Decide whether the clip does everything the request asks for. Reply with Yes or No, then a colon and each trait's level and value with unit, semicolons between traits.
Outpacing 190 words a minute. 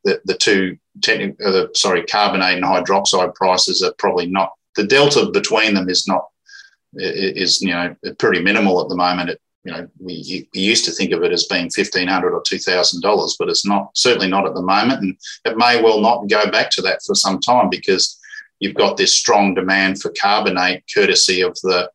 Yes: average, 200 wpm